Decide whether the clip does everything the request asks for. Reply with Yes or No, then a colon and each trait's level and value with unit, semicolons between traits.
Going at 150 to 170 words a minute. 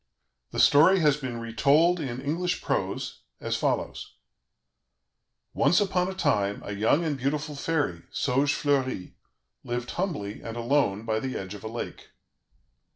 No: average, 140 wpm